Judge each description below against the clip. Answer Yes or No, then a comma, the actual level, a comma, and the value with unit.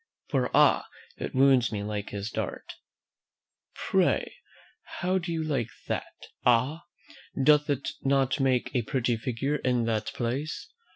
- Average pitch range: Yes, average, 3.7 semitones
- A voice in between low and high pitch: No, low, 130 Hz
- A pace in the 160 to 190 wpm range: No, slow, 135 wpm